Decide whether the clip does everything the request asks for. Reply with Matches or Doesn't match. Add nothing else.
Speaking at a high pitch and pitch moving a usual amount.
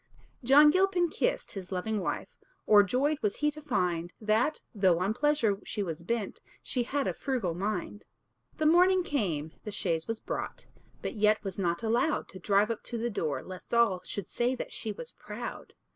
Doesn't match